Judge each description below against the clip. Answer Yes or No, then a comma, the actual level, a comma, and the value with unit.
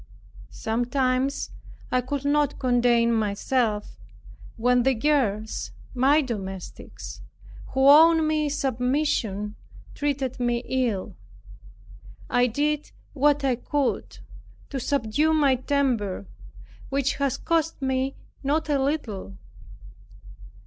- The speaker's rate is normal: No, slow, 100 wpm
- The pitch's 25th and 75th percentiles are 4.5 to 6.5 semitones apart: No, average, 3.6 semitones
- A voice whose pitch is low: No, very high, 260 Hz